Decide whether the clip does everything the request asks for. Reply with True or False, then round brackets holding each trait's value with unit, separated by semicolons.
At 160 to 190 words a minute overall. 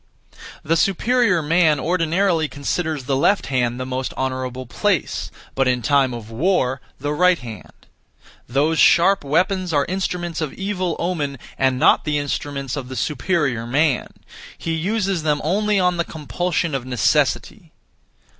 False (145 wpm)